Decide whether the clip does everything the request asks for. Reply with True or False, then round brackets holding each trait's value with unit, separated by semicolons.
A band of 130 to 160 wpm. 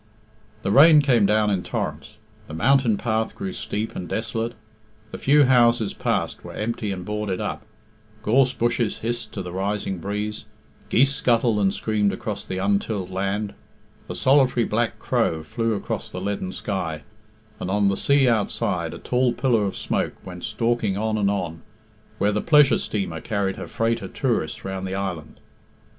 False (170 wpm)